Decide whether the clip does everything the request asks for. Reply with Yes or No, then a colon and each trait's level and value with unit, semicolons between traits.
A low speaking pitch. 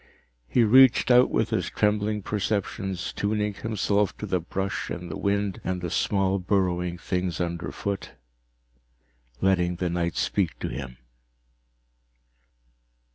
Yes: very low, 95 Hz